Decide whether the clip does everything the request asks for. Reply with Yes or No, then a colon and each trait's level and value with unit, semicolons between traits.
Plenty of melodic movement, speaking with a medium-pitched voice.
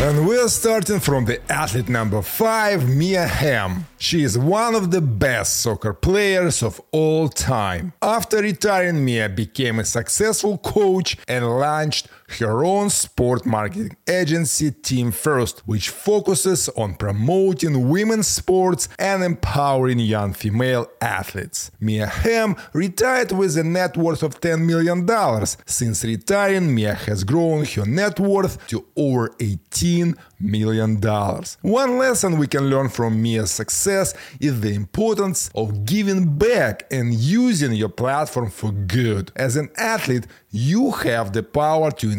Yes: wide, 8.8 semitones; medium, 145 Hz